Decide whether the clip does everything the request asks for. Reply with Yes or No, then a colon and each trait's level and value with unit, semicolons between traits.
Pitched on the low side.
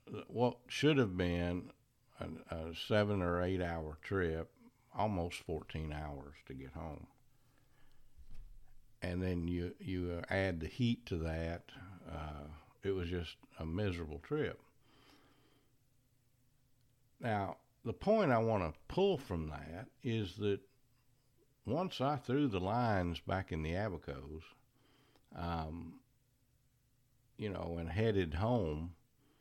Yes: low, 100 Hz